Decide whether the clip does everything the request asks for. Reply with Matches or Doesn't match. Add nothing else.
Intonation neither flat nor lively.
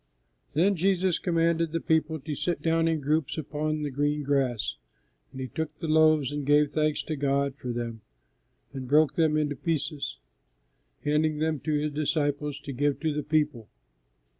Doesn't match